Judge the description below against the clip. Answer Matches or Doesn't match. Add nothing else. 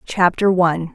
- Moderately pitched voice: Matches